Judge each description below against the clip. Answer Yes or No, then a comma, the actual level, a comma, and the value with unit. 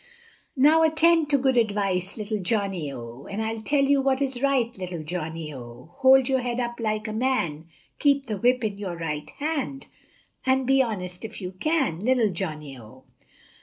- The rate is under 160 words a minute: No, average, 180 wpm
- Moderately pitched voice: No, high, 220 Hz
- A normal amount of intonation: No, wide, 6.9 semitones